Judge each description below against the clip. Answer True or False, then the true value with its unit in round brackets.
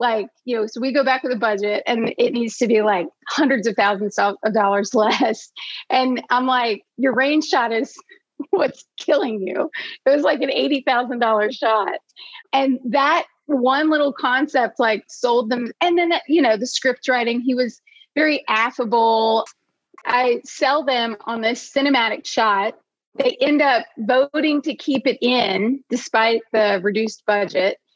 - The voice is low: False (250 Hz)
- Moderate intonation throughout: True (3.9 semitones)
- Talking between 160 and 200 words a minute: True (165 wpm)